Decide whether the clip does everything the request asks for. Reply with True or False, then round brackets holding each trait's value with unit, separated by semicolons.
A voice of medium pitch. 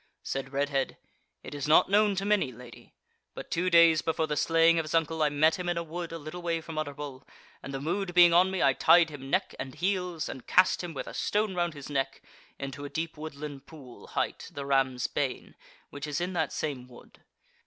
True (155 Hz)